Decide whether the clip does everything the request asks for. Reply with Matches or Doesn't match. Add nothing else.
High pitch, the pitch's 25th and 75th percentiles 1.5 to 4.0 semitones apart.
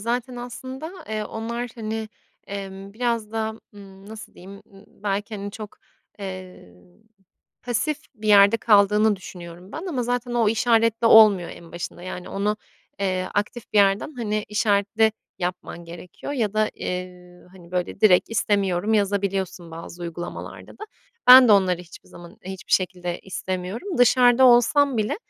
Matches